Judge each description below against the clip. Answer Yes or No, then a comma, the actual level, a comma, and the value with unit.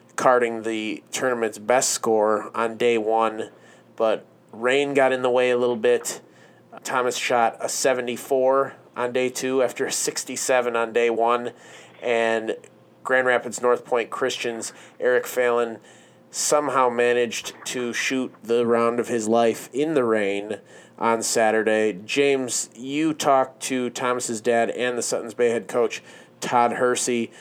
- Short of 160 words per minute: Yes, average, 150 wpm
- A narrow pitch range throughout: Yes, narrow, 1.8 semitones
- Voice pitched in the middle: No, low, 120 Hz